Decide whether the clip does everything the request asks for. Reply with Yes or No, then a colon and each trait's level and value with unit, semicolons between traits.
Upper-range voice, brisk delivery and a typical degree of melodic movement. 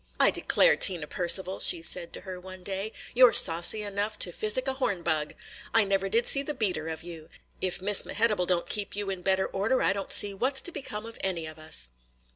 Yes: high, 195 Hz; fast, 230 wpm; average, 3.4 semitones